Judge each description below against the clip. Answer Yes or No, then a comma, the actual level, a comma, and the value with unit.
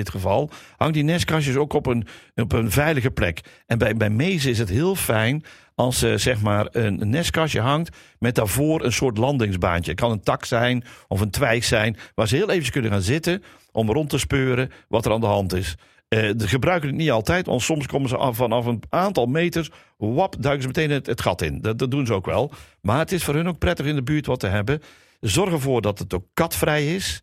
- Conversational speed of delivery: No, fast, 240 wpm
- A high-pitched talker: No, low, 125 Hz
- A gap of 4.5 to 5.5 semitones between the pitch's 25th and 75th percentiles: Yes, average, 5.2 semitones